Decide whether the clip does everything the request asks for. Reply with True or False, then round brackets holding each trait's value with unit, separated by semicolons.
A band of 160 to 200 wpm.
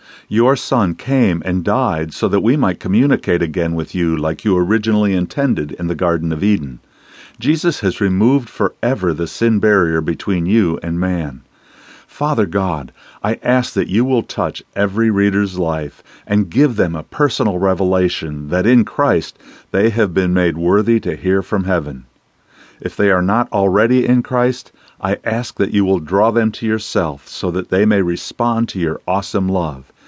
True (175 wpm)